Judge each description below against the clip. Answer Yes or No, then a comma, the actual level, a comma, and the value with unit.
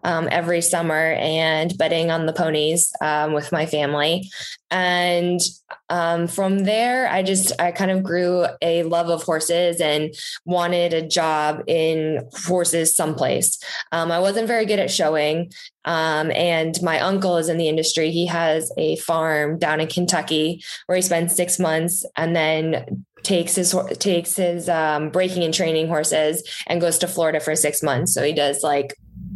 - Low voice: No, medium, 165 Hz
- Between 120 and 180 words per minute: Yes, average, 170 wpm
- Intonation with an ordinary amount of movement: No, narrow, 2.0 semitones